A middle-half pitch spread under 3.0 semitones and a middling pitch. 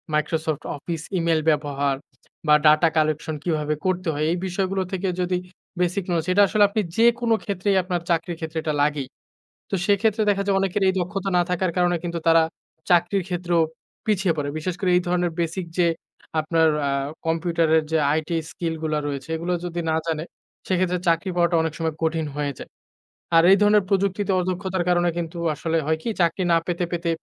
Yes: narrow, 2.6 semitones; medium, 175 Hz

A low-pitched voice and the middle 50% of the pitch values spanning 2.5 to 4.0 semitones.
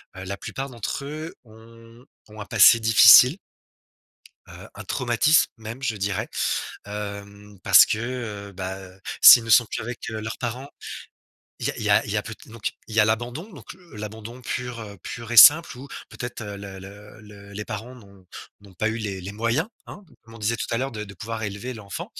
Yes: low, 110 Hz; average, 2.9 semitones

